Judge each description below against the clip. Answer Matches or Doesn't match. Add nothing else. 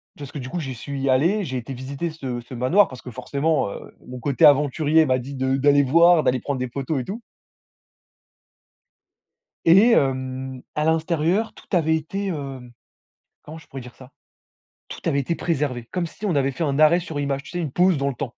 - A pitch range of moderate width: Matches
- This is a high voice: Doesn't match